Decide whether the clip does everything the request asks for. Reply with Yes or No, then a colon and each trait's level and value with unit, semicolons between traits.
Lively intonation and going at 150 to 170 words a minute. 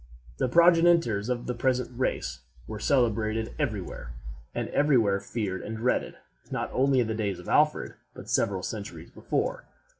No: average, 4.3 semitones; average, 160 wpm